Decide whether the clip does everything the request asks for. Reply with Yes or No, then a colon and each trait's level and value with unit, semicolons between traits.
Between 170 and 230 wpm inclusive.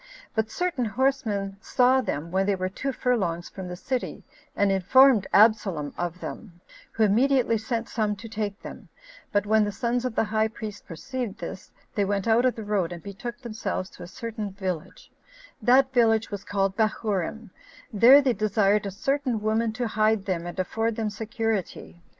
Yes: average, 180 wpm